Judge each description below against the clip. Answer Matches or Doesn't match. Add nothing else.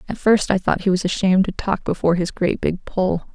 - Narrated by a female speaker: Matches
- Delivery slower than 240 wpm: Doesn't match